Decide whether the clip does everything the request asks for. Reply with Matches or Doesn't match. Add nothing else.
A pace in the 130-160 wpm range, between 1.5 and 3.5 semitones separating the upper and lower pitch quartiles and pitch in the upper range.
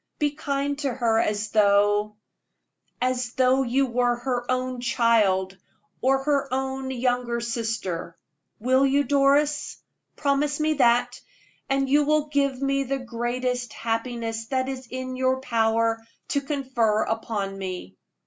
Matches